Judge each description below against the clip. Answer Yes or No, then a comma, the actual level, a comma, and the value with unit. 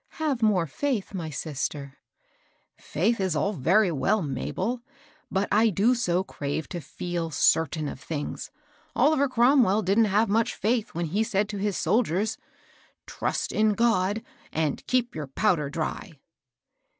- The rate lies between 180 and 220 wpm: No, average, 155 wpm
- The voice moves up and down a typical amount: No, wide, 5.7 semitones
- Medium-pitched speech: No, high, 195 Hz